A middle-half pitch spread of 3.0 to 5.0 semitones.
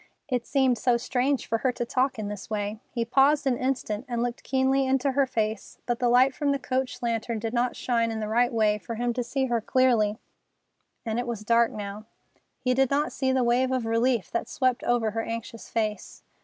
No: narrow, 2.5 semitones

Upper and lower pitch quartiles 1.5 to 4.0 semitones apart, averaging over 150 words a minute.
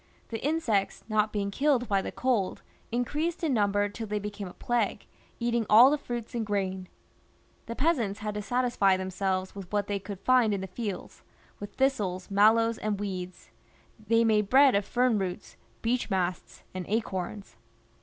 Yes: average, 3.4 semitones; average, 170 wpm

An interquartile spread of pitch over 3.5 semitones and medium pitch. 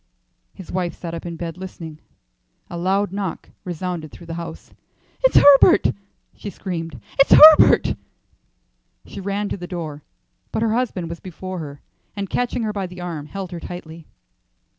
No: average, 3.1 semitones; medium, 180 Hz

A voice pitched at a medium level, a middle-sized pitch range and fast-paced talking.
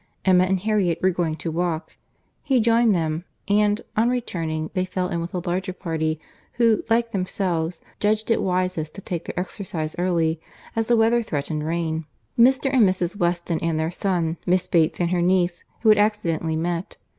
No: medium, 180 Hz; average, 4.0 semitones; average, 180 wpm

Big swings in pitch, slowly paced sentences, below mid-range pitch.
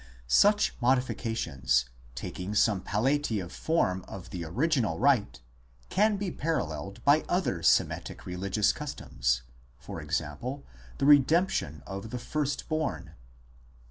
Yes: wide, 8.4 semitones; slow, 110 wpm; low, 110 Hz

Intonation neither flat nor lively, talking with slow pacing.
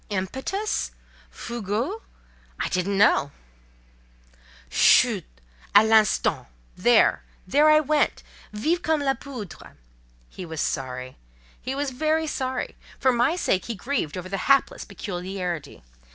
No: wide, 7.5 semitones; slow, 110 wpm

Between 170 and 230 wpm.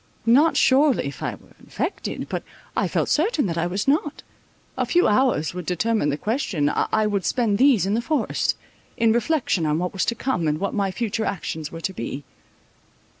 Yes: average, 185 wpm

